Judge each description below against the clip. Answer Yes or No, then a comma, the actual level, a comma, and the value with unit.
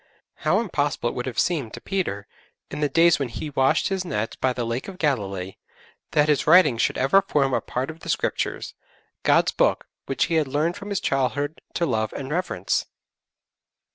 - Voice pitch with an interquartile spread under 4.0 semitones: No, average, 5.0 semitones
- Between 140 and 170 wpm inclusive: No, average, 195 wpm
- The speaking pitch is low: No, medium, 145 Hz